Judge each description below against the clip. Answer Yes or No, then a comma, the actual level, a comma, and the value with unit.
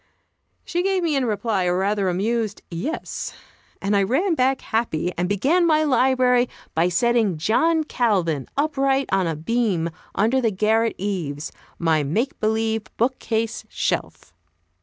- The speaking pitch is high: Yes, high, 225 Hz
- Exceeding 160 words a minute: No, average, 145 wpm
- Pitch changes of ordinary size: No, wide, 6.0 semitones